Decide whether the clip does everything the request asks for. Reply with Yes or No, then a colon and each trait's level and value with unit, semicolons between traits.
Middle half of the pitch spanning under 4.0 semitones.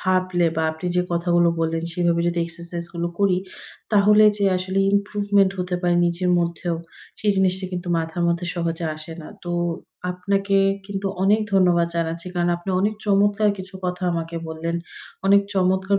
Yes: narrow, 2.4 semitones